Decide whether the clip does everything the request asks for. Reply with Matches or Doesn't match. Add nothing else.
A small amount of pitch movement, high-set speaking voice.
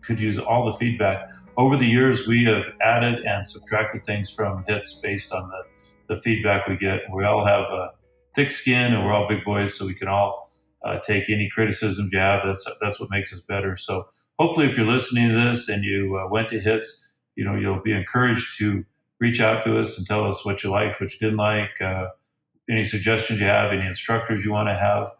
Doesn't match